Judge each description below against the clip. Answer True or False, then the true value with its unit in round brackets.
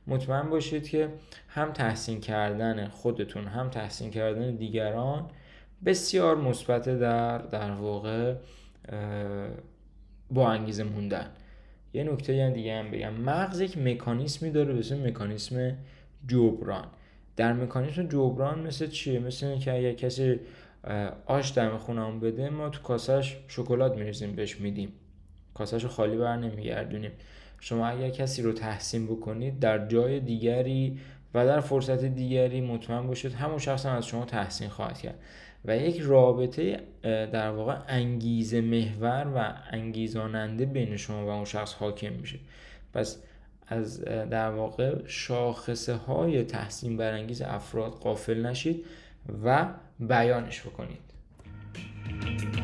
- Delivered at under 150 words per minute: True (125 wpm)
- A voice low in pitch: True (120 Hz)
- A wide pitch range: False (3.3 semitones)